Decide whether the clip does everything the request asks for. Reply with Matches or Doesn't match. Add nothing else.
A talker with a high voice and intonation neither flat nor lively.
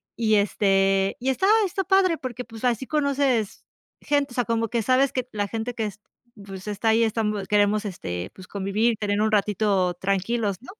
Matches